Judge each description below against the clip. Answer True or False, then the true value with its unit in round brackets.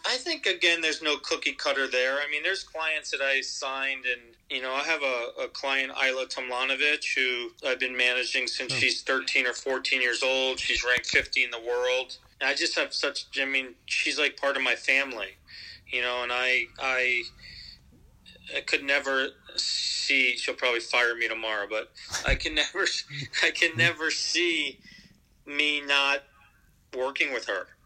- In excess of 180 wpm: False (175 wpm)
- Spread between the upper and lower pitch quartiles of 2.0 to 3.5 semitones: True (3.1 semitones)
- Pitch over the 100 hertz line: True (135 Hz)